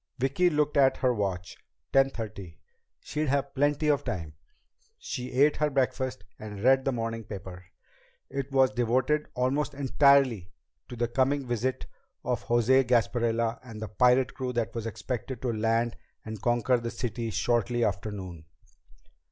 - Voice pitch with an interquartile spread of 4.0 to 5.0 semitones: No, average, 3.0 semitones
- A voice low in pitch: Yes, low, 125 Hz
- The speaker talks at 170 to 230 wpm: No, average, 155 wpm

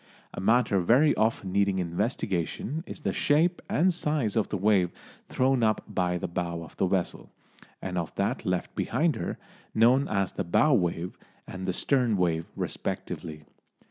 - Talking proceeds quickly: No, average, 165 wpm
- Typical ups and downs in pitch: No, wide, 6.3 semitones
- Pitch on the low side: Yes, low, 100 Hz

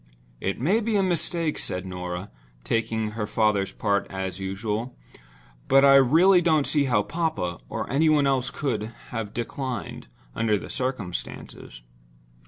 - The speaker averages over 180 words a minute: No, average, 145 wpm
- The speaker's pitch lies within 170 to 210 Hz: No, low, 120 Hz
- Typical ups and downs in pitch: No, wide, 6.6 semitones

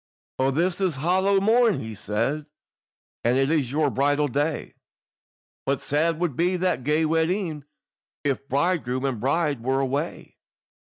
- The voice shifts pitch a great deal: No, average, 4.2 semitones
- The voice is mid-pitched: Yes, medium, 150 Hz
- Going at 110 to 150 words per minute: Yes, average, 140 wpm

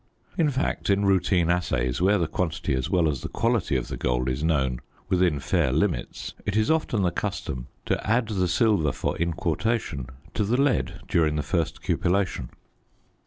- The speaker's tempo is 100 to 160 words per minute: No, average, 175 wpm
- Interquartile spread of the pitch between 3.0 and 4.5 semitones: No, average, 5.2 semitones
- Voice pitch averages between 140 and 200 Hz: No, very low, 90 Hz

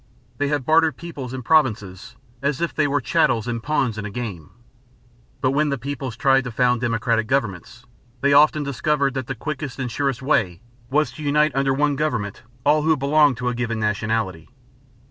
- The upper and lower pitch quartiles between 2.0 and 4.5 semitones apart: Yes, average, 4.1 semitones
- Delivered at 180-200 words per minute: Yes, average, 185 wpm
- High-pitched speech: No, low, 135 Hz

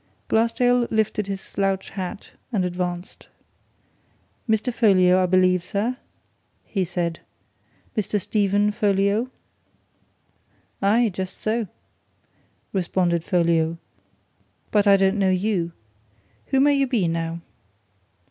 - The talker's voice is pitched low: No, high, 195 Hz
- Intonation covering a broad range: No, average, 3.2 semitones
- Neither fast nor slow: No, slow, 105 wpm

